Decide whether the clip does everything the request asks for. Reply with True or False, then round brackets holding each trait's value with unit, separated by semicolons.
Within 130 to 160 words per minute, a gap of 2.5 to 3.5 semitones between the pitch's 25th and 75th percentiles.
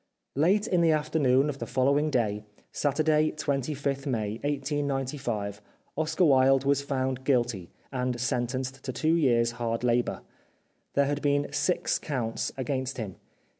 True (135 wpm; 2.9 semitones)